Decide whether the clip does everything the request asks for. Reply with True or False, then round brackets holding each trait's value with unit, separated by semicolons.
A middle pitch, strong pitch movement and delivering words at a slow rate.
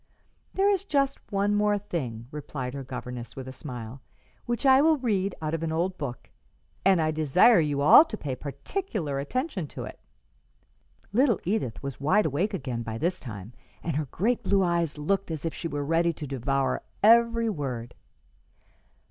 False (160 Hz; 7.2 semitones; 175 wpm)